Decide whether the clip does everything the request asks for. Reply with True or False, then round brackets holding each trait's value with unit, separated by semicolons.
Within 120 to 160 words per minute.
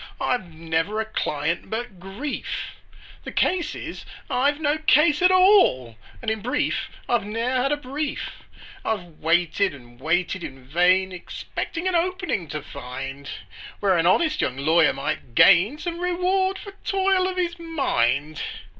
True (150 wpm)